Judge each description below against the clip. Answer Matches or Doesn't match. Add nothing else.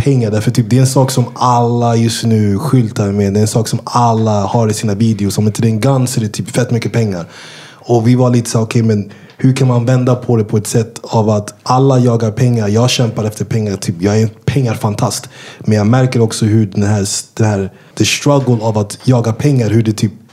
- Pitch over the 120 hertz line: Doesn't match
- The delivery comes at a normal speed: Doesn't match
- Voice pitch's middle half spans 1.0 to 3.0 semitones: Matches